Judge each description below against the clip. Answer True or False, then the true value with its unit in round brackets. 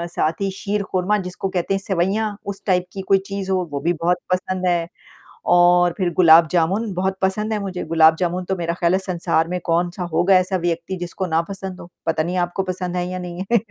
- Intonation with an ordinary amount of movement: False (1.7 semitones)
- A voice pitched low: False (180 Hz)